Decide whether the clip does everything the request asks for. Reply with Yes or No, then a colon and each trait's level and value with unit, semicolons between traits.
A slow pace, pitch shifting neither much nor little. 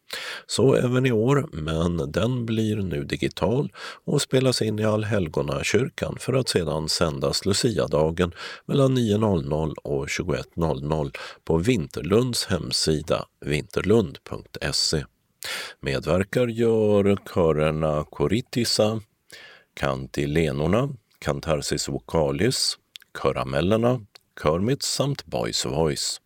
No: slow, 90 wpm; wide, 7.7 semitones